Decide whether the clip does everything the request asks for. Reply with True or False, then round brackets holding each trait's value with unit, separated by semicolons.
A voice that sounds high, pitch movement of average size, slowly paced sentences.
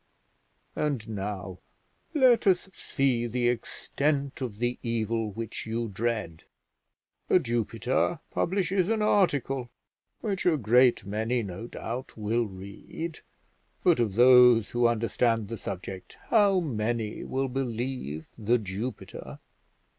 False (120 Hz; 3.8 semitones; 115 wpm)